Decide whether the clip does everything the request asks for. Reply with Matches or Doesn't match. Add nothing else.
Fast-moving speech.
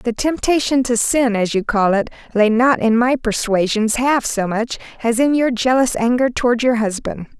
Doesn't match